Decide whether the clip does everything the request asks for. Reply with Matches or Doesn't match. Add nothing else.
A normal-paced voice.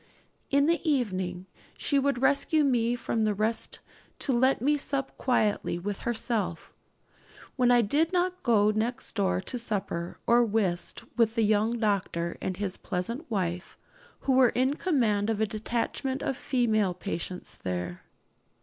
Matches